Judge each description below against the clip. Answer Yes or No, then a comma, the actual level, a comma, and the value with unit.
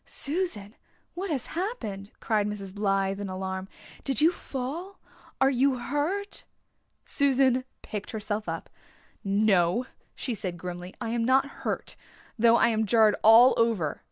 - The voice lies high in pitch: Yes, high, 230 Hz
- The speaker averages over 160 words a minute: No, average, 140 wpm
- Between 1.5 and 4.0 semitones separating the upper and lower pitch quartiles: No, wide, 5.4 semitones